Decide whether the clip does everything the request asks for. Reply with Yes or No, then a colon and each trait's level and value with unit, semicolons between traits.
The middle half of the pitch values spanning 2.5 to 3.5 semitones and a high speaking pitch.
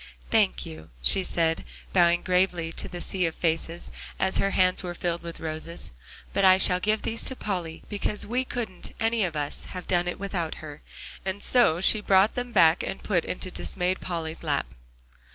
No: average, 2.9 semitones; medium, 180 Hz